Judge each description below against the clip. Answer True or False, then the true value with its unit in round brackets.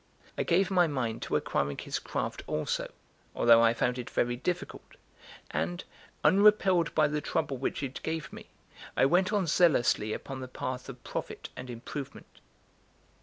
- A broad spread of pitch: True (6.1 semitones)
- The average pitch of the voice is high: False (135 Hz)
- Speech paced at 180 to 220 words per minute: False (160 wpm)